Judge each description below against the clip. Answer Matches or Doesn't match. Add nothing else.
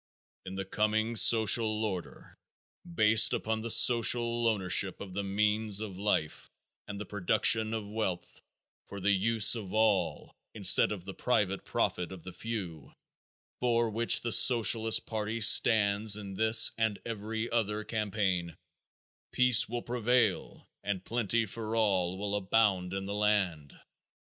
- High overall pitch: Doesn't match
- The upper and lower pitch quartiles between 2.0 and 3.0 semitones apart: Matches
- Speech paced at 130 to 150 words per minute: Matches